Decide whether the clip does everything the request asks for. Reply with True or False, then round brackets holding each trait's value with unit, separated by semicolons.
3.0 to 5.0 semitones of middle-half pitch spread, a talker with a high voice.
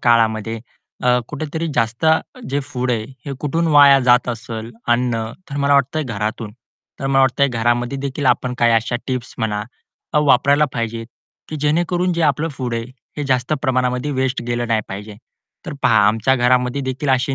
False (3.4 semitones; 125 Hz)